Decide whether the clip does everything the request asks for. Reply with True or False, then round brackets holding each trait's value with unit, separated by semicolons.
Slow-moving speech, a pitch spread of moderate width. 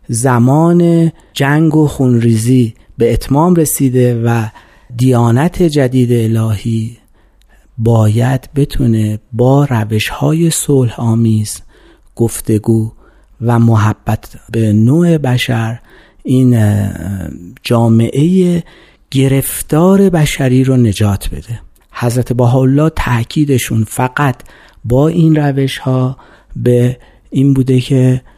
True (95 wpm; 3.6 semitones)